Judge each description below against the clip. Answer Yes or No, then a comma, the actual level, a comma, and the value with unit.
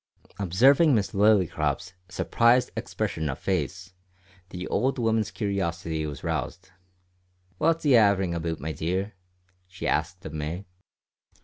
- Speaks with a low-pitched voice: Yes, very low, 95 Hz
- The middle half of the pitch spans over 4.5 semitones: Yes, average, 4.9 semitones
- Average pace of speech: No, slow, 120 wpm